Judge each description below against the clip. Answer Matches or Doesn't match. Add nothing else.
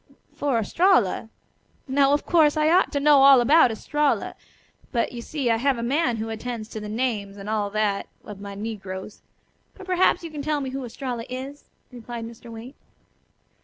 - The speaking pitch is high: Matches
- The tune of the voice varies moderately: Matches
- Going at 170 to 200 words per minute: Matches